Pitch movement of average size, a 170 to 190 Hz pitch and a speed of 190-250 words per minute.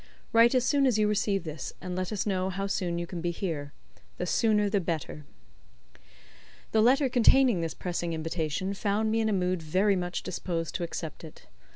Yes: average, 4.1 semitones; medium, 185 Hz; average, 195 wpm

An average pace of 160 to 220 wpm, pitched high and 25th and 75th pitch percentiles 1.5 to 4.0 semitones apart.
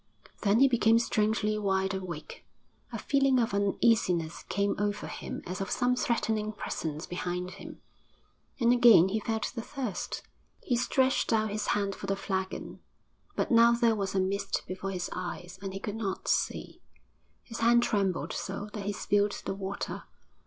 Yes: average, 165 wpm; high, 205 Hz; average, 3.2 semitones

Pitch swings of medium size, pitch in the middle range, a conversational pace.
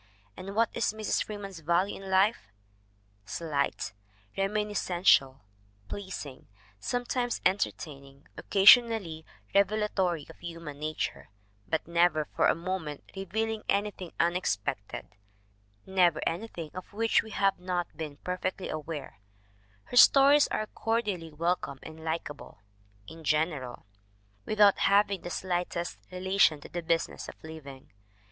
No: average, 4.1 semitones; medium, 180 Hz; slow, 125 wpm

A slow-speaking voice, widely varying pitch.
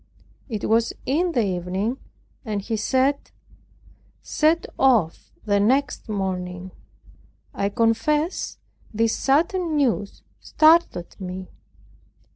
Yes: slow, 95 wpm; wide, 6.3 semitones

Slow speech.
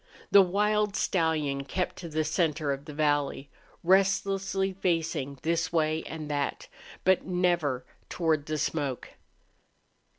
Yes: slow, 125 wpm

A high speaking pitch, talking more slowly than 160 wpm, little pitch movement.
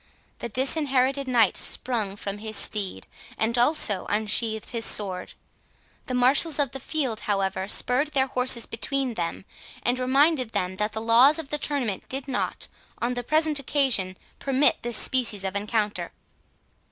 No: high, 245 Hz; average, 150 wpm; average, 4.4 semitones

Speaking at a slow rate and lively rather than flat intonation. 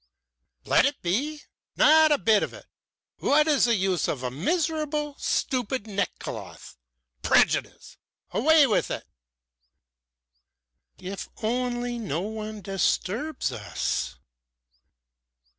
Yes: slow, 105 wpm; wide, 7.2 semitones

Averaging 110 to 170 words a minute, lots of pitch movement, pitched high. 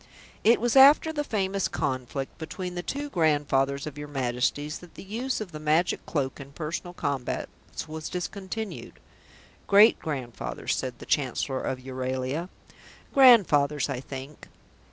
No: average, 140 wpm; wide, 6.3 semitones; medium, 150 Hz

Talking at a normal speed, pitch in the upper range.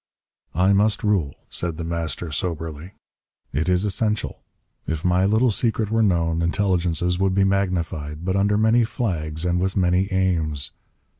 No: average, 150 wpm; very low, 90 Hz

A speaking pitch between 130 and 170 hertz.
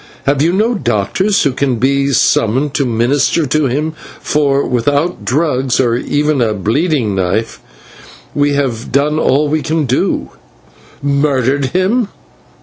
Yes: medium, 140 Hz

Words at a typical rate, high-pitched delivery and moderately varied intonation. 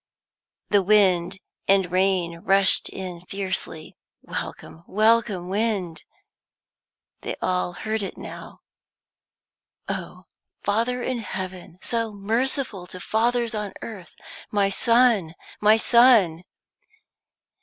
No: slow, 100 wpm; high, 200 Hz; average, 3.7 semitones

